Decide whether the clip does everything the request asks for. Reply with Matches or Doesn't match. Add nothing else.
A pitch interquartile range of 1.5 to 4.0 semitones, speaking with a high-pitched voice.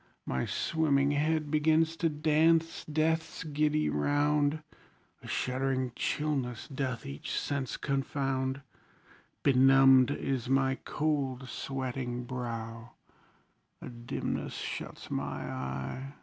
Doesn't match